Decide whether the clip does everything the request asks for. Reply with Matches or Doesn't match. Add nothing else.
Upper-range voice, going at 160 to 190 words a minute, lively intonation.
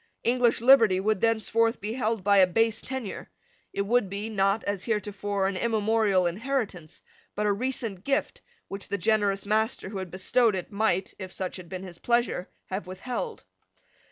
Doesn't match